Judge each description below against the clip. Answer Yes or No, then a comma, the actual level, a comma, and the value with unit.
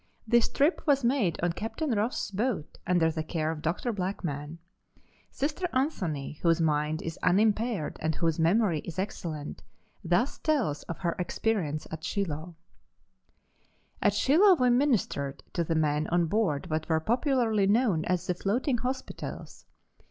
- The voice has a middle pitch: Yes, medium, 180 Hz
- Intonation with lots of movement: Yes, wide, 6.8 semitones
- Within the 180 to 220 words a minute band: No, average, 145 wpm